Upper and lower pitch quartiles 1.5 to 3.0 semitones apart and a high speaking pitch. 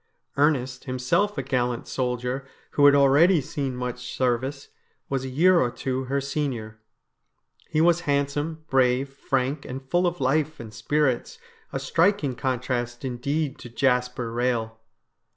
No: narrow, 2.6 semitones; low, 135 Hz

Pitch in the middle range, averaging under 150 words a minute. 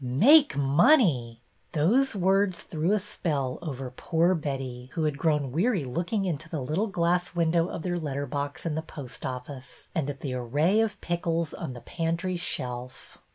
No: medium, 160 Hz; average, 175 wpm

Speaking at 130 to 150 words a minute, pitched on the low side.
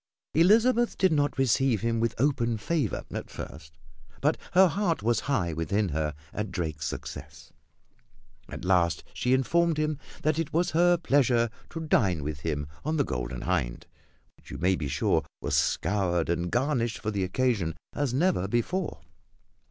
No: average, 160 wpm; low, 120 Hz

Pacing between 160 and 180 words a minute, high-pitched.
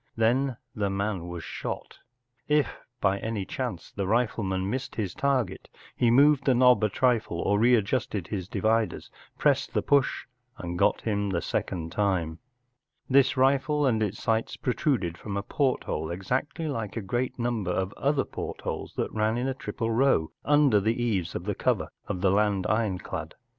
No: average, 170 wpm; low, 110 Hz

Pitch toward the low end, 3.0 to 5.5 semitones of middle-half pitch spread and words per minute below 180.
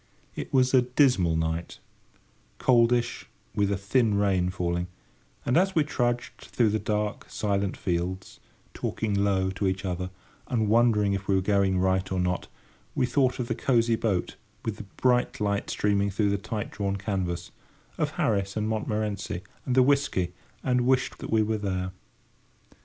Yes: low, 105 Hz; average, 4.0 semitones; average, 165 wpm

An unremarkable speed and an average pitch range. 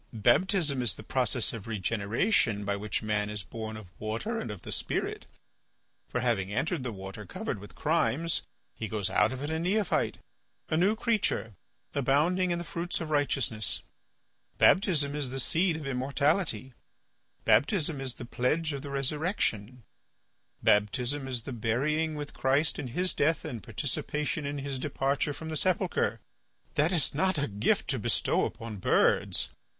No: average, 160 wpm; wide, 6.0 semitones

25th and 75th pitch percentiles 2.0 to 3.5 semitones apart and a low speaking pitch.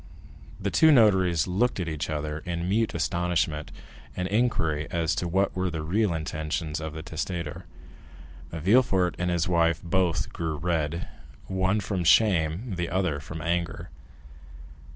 Yes: average, 3.0 semitones; very low, 85 Hz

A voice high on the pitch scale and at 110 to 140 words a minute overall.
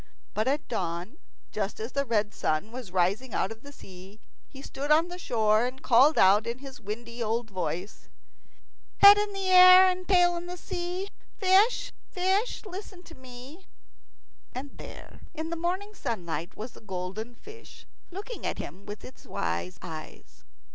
No: very high, 255 Hz; average, 160 wpm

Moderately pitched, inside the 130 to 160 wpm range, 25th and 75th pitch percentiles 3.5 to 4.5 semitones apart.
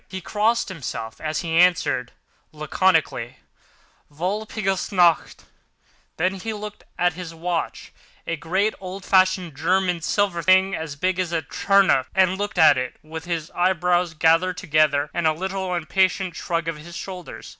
No: medium, 175 Hz; average, 150 wpm; average, 2.7 semitones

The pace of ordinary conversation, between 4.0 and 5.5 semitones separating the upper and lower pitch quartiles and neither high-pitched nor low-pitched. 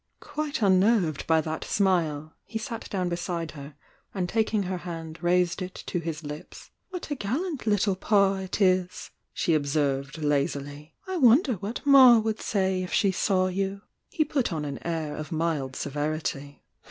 Yes: average, 170 wpm; average, 5.1 semitones; medium, 180 Hz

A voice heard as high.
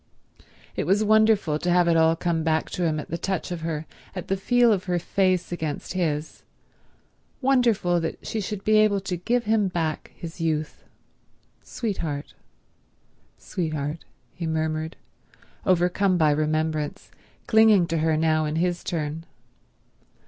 No: medium, 170 Hz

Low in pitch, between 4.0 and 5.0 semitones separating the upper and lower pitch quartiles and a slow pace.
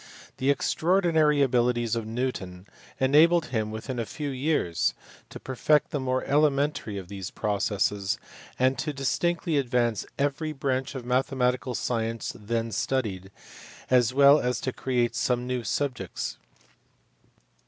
No: low, 130 Hz; average, 3.6 semitones; slow, 130 wpm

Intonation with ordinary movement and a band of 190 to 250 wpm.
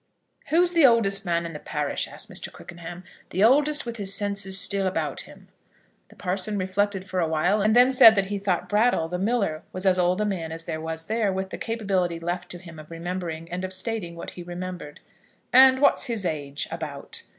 Yes: average, 3.8 semitones; fast, 205 wpm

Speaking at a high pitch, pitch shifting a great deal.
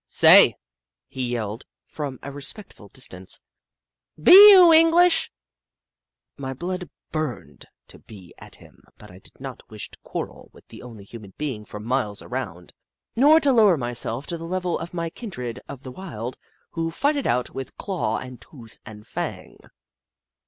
No: low, 135 Hz; wide, 8.1 semitones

